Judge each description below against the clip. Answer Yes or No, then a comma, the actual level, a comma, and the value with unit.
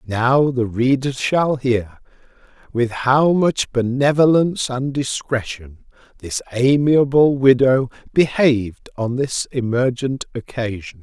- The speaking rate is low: Yes, slow, 105 wpm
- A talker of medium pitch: No, low, 130 Hz